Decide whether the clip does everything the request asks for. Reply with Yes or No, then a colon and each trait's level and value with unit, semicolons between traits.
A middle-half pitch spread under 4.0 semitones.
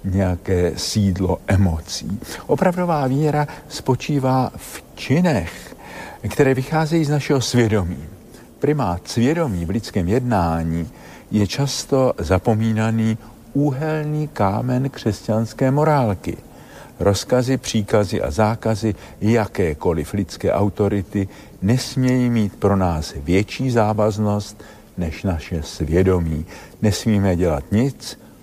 No: wide, 5.6 semitones